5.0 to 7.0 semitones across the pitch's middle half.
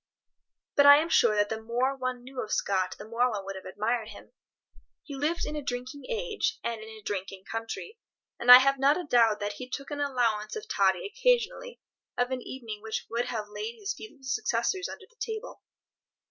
Yes: wide, 5.5 semitones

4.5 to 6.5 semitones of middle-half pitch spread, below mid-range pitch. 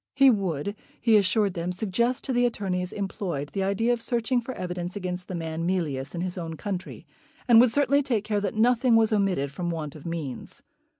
No: average, 4.8 semitones; high, 195 Hz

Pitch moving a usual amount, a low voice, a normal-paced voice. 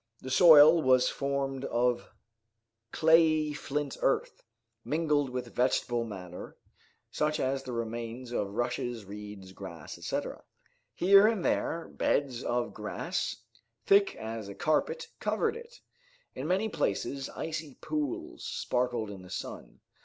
No: average, 5.0 semitones; low, 130 Hz; slow, 125 wpm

